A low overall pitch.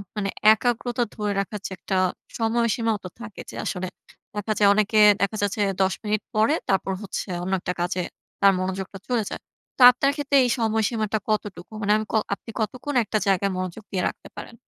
No: high, 210 Hz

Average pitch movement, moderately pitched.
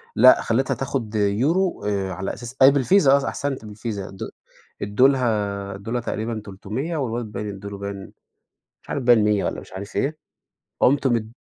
No: average, 4.7 semitones; low, 110 Hz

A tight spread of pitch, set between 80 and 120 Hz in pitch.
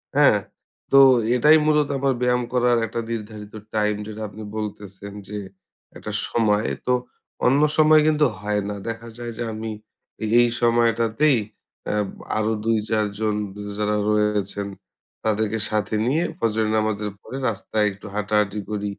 Yes: narrow, 2.2 semitones; low, 110 Hz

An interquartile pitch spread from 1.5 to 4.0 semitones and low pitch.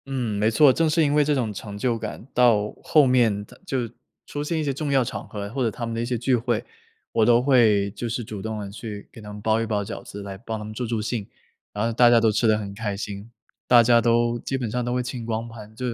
Yes: average, 2.7 semitones; low, 115 Hz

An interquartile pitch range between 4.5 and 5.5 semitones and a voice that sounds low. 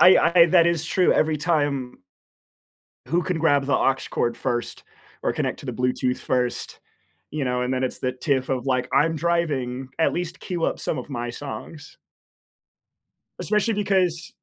No: average, 5.0 semitones; medium, 145 Hz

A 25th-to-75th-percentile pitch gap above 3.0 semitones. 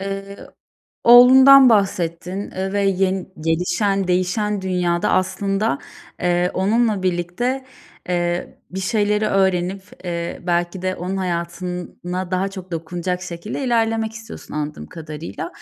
No: narrow, 2.5 semitones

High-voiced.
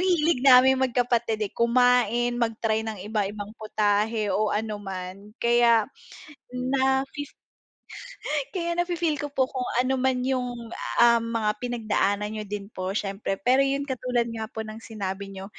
Yes: high, 235 Hz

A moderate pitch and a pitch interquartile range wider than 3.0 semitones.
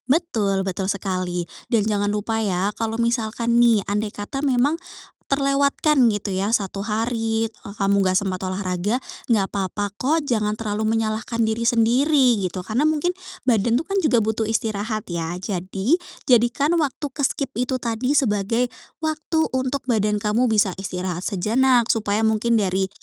No: high, 220 Hz; average, 3.8 semitones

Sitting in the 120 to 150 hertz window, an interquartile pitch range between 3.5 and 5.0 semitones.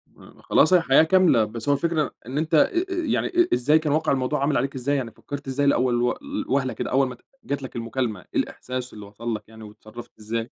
Yes: low, 135 Hz; average, 4.4 semitones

